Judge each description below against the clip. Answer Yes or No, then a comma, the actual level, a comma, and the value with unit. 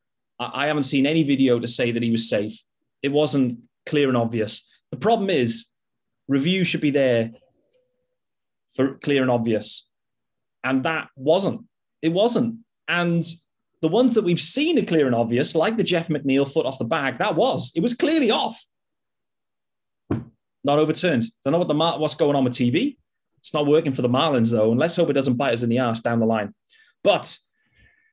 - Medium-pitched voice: Yes, medium, 145 Hz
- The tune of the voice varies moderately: No, wide, 6.0 semitones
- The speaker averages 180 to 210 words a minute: Yes, average, 190 wpm